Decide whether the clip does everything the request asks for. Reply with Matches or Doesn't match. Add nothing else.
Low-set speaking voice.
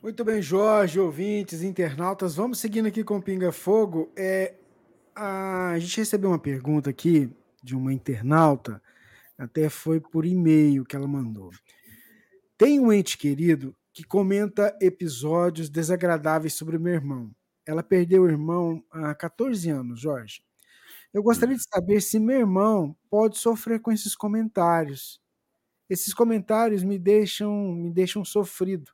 Doesn't match